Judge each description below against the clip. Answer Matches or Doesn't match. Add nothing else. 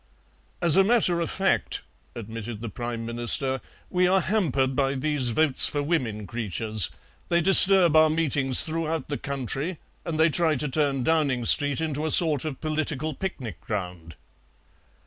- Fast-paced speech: Doesn't match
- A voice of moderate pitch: Matches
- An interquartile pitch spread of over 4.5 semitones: Matches